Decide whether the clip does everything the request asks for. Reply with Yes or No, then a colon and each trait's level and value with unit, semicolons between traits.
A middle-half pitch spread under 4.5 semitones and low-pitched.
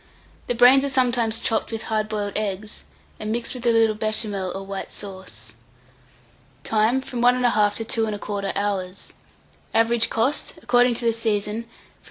No: narrow, 2.5 semitones; high, 220 Hz